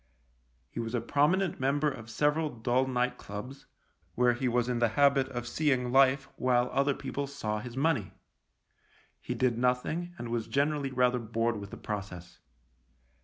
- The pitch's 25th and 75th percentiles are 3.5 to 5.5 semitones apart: No, average, 3.0 semitones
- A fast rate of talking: No, average, 165 wpm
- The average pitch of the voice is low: Yes, low, 125 Hz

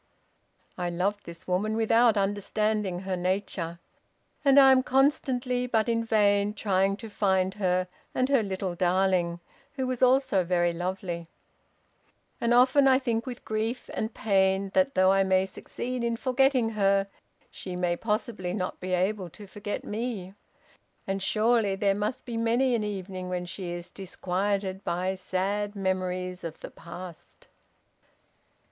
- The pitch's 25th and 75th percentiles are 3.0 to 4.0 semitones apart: Yes, average, 3.7 semitones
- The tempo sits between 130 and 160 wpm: Yes, average, 150 wpm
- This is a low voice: No, high, 200 Hz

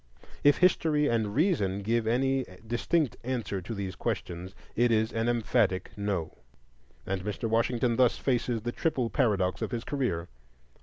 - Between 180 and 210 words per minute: No, average, 155 wpm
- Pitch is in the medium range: No, low, 115 Hz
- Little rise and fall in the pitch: No, average, 4.1 semitones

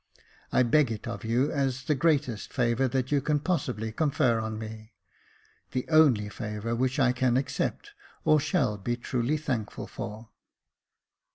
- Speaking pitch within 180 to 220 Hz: No, low, 125 Hz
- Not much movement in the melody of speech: No, average, 4.1 semitones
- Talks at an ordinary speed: Yes, average, 160 wpm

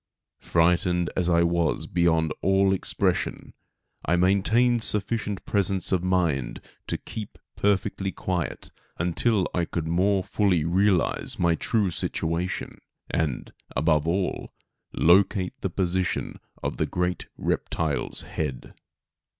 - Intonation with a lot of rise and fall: No, narrow, 2.5 semitones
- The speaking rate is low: Yes, slow, 115 wpm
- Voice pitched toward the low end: Yes, very low, 90 Hz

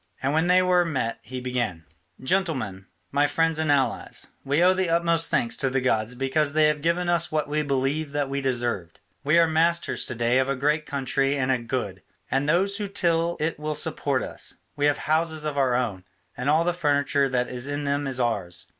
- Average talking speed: No, fast, 215 wpm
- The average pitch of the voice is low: No, medium, 145 Hz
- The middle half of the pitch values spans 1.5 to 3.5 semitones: No, average, 4.0 semitones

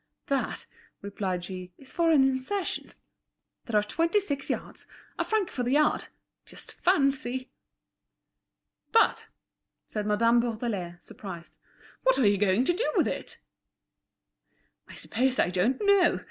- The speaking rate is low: Yes, slow, 130 wpm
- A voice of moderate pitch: No, very high, 250 Hz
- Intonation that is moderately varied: No, wide, 7.0 semitones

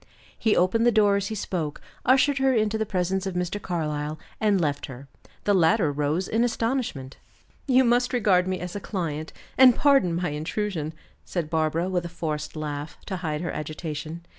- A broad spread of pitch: Yes, wide, 5.7 semitones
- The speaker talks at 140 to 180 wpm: No, average, 190 wpm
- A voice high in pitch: No, medium, 180 Hz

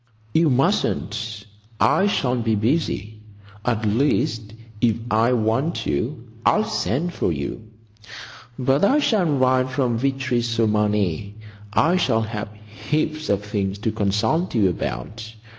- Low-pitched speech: Yes, low, 115 Hz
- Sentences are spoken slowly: Yes, slow, 130 wpm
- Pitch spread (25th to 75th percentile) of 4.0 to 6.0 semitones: Yes, average, 4.5 semitones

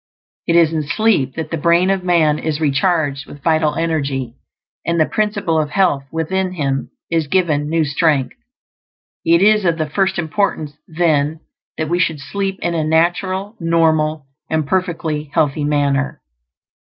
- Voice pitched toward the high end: No, medium, 160 Hz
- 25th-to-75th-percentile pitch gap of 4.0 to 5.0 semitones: No, average, 2.8 semitones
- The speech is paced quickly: No, average, 155 wpm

